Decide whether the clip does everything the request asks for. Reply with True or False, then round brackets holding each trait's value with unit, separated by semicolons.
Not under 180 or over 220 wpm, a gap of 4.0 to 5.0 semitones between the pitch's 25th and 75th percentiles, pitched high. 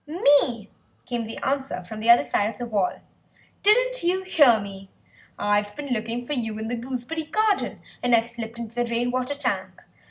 True (190 wpm; 4.4 semitones; 240 Hz)